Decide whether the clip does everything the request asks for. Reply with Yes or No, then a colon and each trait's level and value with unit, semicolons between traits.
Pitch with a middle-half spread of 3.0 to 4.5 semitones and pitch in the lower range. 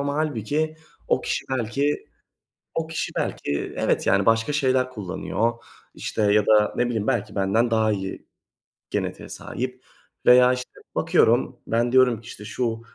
Yes: average, 3.5 semitones; low, 120 Hz